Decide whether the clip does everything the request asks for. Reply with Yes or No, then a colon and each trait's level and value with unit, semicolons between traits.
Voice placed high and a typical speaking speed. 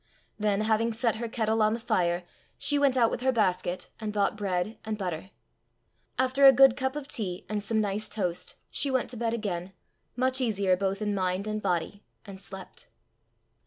Yes: high, 215 Hz; average, 190 wpm